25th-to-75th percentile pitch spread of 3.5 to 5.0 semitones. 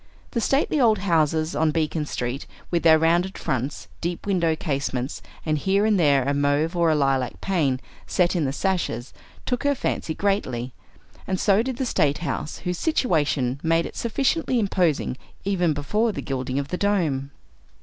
No: wide, 5.6 semitones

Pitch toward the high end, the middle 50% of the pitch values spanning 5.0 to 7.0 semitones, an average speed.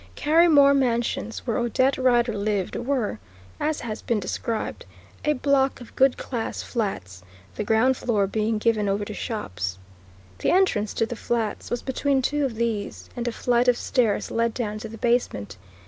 No: high, 235 Hz; average, 3.5 semitones; average, 170 wpm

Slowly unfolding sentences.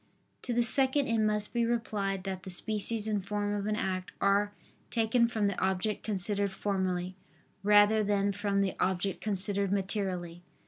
No: average, 165 wpm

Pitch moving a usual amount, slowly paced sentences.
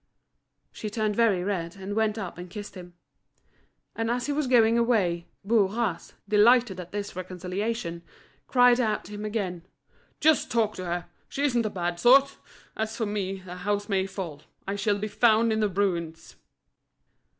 No: average, 3.6 semitones; average, 170 wpm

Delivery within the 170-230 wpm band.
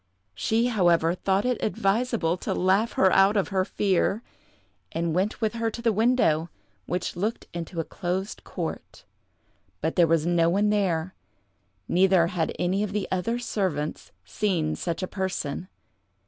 No: average, 155 wpm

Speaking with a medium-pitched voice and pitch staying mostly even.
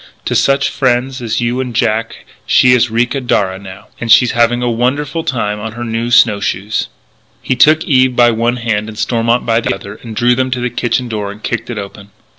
No: low, 120 Hz; narrow, 2.1 semitones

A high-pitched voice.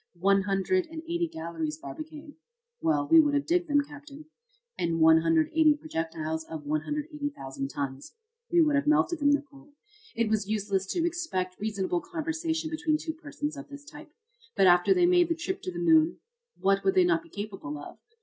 Yes: very high, 290 Hz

